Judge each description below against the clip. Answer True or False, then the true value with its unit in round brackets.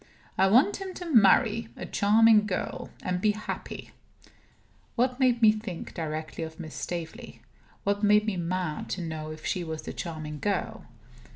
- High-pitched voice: True (195 Hz)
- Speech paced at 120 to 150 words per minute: False (165 wpm)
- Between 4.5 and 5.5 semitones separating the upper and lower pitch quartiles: True (5.2 semitones)